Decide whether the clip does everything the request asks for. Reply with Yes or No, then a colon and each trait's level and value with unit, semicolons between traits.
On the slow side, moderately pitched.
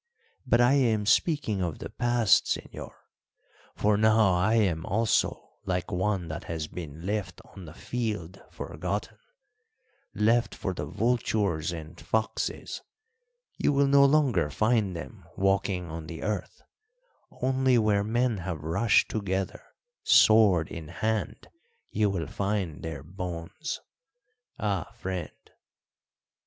No: slow, 125 wpm; low, 100 Hz